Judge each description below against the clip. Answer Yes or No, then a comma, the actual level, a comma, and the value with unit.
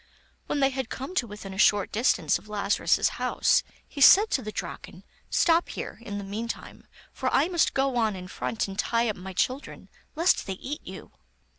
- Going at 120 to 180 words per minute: No, average, 195 wpm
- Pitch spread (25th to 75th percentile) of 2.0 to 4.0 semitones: No, average, 5.1 semitones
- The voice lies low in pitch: No, high, 230 Hz